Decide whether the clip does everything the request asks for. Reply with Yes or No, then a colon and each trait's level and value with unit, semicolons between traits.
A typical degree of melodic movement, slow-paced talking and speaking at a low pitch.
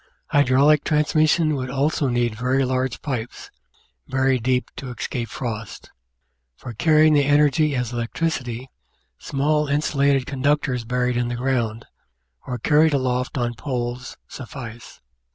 Yes: average, 3.0 semitones; slow, 125 wpm; low, 130 Hz